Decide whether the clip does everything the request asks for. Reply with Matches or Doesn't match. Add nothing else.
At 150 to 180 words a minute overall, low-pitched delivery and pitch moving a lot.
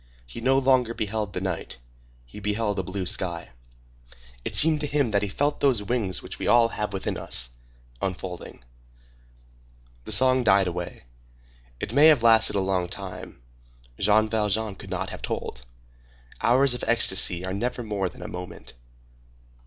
Doesn't match